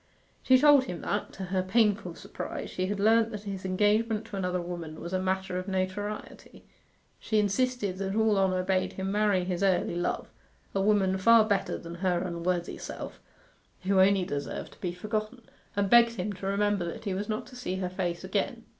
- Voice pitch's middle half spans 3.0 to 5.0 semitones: No, narrow, 2.5 semitones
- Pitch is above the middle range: Yes, high, 195 Hz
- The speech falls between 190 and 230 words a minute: Yes, average, 195 wpm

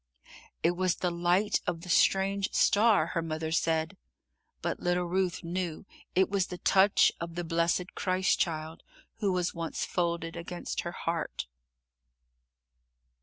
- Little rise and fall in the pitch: Yes, narrow, 1.9 semitones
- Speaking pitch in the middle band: Yes, medium, 175 Hz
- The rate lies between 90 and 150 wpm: Yes, average, 140 wpm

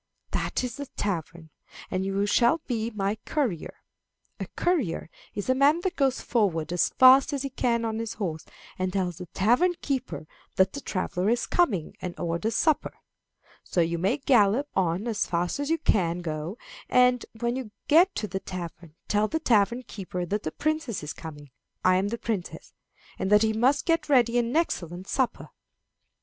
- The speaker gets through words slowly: No, average, 180 wpm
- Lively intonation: Yes, wide, 6.2 semitones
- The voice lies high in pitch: Yes, high, 215 Hz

